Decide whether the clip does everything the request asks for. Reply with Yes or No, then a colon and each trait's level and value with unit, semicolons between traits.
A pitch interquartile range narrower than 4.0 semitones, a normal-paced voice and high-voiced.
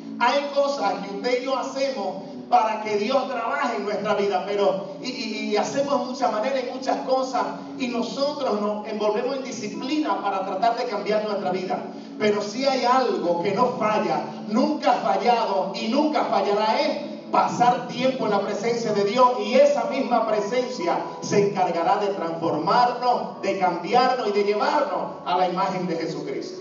No: average, 4.3 semitones; average, 170 wpm; high, 230 Hz